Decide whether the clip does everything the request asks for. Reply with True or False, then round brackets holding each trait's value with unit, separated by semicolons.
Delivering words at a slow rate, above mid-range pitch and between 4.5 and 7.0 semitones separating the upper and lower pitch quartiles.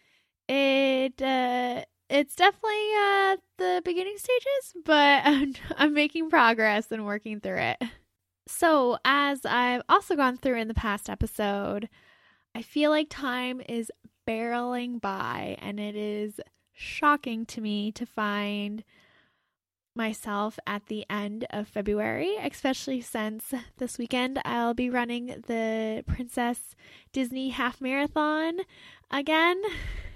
True (125 wpm; 250 Hz; 5.1 semitones)